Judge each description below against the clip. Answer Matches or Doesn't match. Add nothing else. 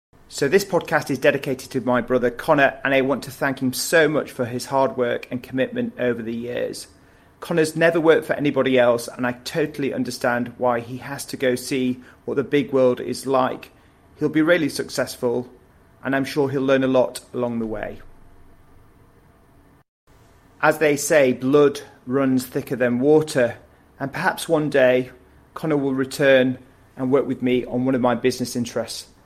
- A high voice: Doesn't match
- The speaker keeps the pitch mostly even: Matches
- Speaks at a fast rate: Doesn't match